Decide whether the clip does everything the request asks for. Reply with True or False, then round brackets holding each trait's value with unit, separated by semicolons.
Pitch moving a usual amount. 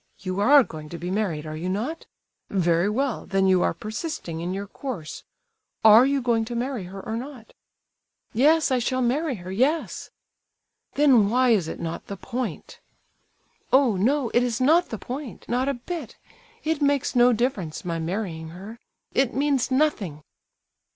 False (6.2 semitones)